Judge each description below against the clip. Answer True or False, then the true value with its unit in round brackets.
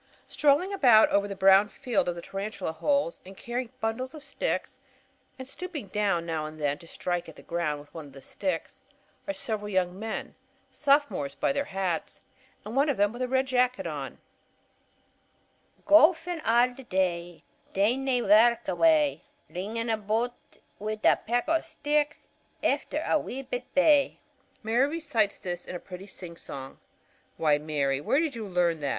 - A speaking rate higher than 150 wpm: True (170 wpm)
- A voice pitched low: False (210 Hz)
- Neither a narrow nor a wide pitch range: False (6.9 semitones)